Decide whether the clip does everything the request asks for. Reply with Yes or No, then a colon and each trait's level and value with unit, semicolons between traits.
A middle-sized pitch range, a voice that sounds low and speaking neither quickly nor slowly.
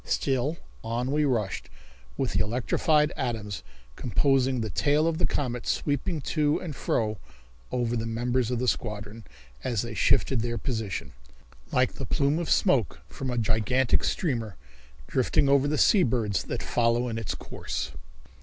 Yes: average, 3.8 semitones; low, 125 Hz; average, 155 wpm